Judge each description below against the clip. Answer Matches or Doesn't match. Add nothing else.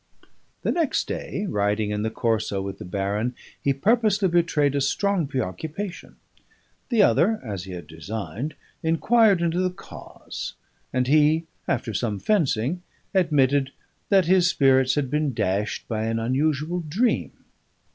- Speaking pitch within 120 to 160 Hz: Matches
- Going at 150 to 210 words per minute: Doesn't match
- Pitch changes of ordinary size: Doesn't match